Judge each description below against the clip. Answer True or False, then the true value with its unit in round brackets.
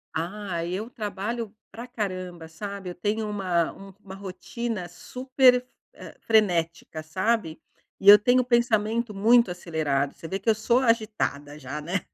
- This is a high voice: True (200 Hz)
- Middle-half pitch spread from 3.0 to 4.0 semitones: False (4.7 semitones)